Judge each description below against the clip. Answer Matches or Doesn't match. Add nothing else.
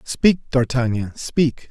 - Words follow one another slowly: Matches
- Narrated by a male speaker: Matches